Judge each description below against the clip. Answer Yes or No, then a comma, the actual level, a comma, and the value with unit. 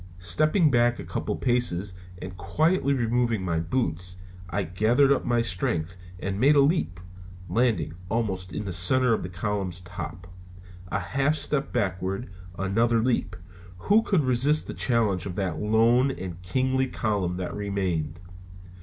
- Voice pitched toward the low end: Yes, low, 105 Hz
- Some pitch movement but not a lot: No, wide, 5.9 semitones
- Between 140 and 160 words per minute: Yes, average, 155 wpm